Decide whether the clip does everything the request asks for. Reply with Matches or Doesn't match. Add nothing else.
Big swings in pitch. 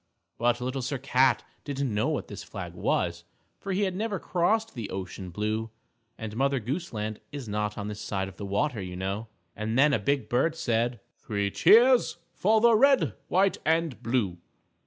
Matches